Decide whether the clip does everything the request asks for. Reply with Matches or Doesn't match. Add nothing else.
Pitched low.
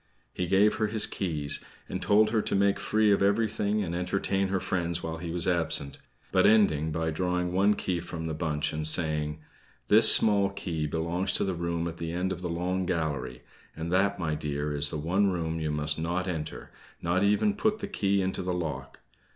Matches